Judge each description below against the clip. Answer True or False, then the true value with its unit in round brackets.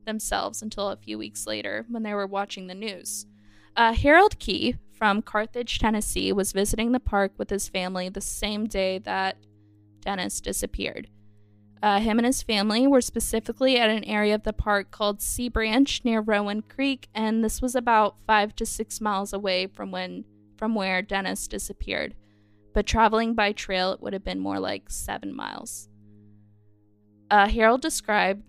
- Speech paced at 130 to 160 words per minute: False (170 wpm)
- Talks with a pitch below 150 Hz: False (205 Hz)